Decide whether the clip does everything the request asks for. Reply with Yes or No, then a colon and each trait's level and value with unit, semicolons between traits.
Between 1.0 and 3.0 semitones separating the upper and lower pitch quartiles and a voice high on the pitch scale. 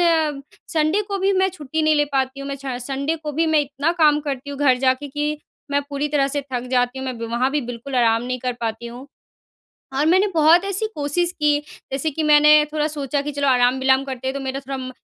Yes: average, 2.7 semitones; very high, 285 Hz